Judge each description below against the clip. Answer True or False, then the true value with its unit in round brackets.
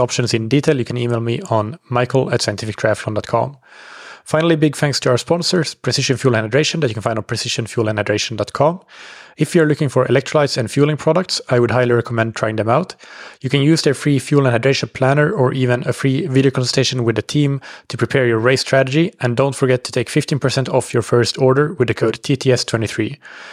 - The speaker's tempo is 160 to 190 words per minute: False (205 wpm)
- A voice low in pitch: True (130 Hz)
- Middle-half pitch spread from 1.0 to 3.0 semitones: False (3.5 semitones)